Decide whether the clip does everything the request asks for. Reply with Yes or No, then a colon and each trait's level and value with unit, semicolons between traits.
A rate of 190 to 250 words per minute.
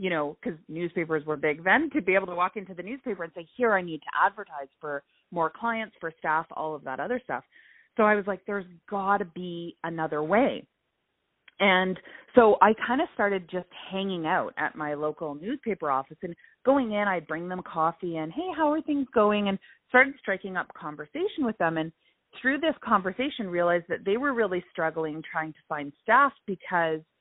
Yes: average, 200 wpm